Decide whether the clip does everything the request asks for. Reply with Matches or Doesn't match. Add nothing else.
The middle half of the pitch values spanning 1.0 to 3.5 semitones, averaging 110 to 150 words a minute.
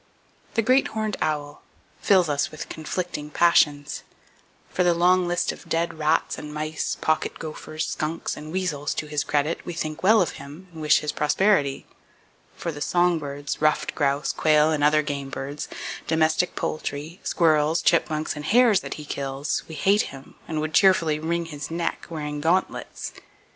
Doesn't match